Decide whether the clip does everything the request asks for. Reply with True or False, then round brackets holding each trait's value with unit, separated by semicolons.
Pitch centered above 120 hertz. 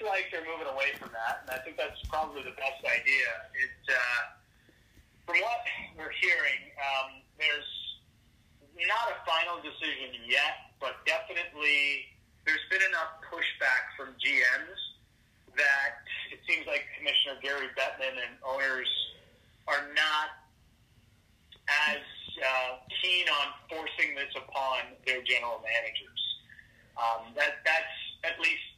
True (135 Hz)